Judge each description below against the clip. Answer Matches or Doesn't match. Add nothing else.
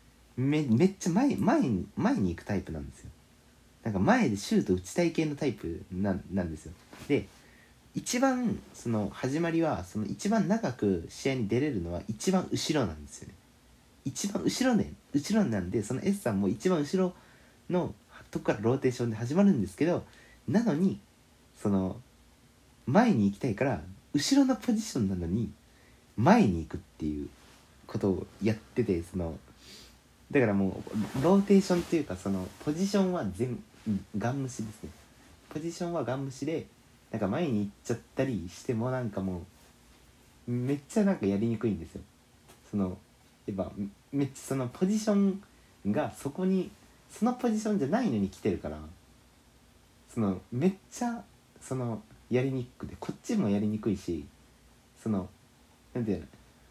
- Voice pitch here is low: Matches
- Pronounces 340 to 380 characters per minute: Doesn't match